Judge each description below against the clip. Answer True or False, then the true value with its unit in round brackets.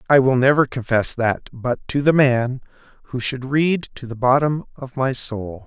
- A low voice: True (130 Hz)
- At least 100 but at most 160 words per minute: False (180 wpm)